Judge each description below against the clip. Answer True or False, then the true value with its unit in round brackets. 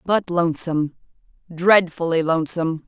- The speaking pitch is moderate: True (170 Hz)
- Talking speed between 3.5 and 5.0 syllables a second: False (5.3 syllables/s)